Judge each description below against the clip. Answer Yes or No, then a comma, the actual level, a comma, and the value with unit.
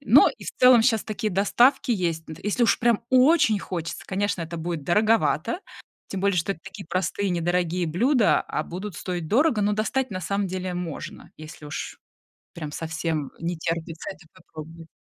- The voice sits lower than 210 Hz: Yes, medium, 185 Hz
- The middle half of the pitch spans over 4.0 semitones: Yes, average, 4.4 semitones